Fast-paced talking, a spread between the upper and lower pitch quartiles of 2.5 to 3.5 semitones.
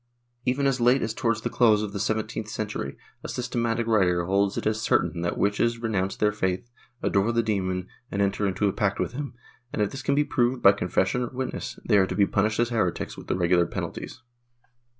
Yes: fast, 215 wpm; average, 3.2 semitones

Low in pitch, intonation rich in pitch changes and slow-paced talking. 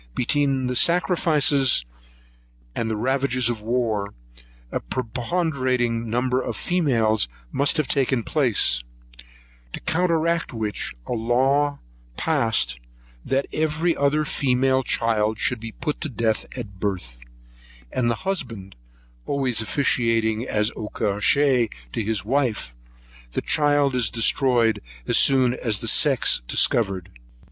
No: low, 125 Hz; average, 4.2 semitones; slow, 120 wpm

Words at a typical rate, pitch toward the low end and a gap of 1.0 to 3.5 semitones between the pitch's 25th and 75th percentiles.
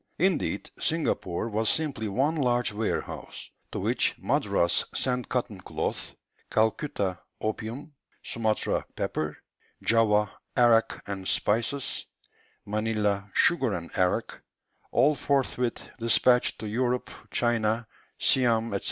No: slow, 105 wpm; low, 115 Hz; average, 3.2 semitones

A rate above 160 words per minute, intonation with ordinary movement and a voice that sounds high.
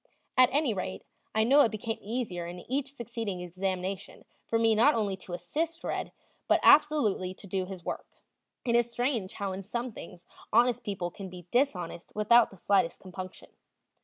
Yes: average, 175 wpm; average, 4.5 semitones; high, 210 Hz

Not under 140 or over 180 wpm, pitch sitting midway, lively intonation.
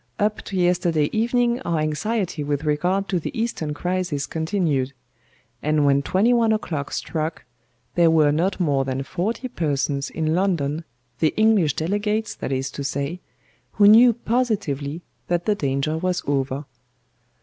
Yes: average, 150 wpm; medium, 165 Hz; wide, 5.8 semitones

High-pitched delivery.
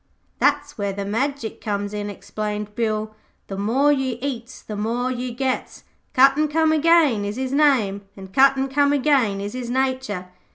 Yes: high, 245 Hz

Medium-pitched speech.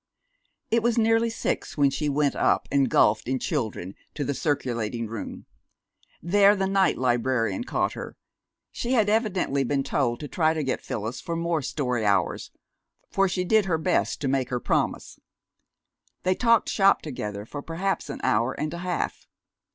Yes: medium, 150 Hz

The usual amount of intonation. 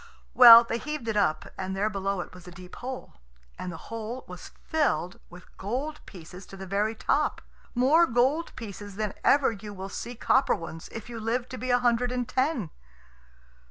Yes: average, 4.6 semitones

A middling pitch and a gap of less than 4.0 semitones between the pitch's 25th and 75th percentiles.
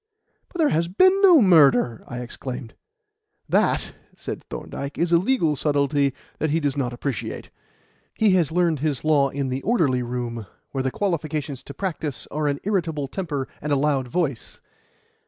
No: medium, 145 Hz; average, 4.3 semitones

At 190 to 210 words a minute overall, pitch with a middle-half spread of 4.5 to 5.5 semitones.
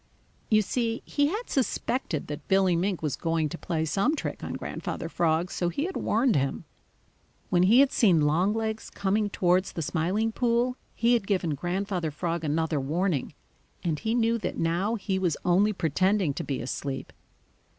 No: average, 170 wpm; average, 5.2 semitones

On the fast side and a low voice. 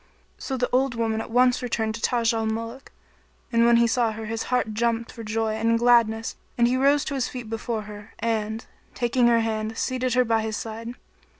No: fast, 215 wpm; high, 230 Hz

